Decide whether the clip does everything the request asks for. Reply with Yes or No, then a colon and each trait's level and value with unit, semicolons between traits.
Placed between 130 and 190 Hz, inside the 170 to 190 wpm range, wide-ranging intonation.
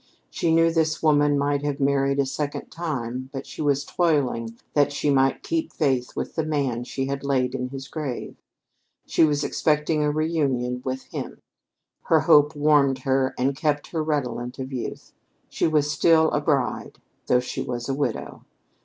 No: medium, 140 Hz; average, 175 wpm; narrow, 2.5 semitones